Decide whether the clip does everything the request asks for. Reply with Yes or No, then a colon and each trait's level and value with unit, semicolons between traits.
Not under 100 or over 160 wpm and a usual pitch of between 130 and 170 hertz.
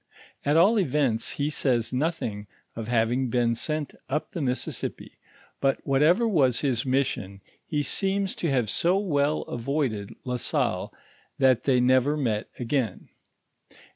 Yes: average, 140 wpm; low, 135 Hz